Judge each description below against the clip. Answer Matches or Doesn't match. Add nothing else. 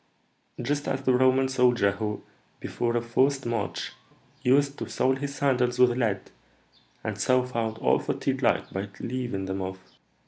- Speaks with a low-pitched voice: Matches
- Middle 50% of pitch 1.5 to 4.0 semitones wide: Matches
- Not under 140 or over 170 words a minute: Matches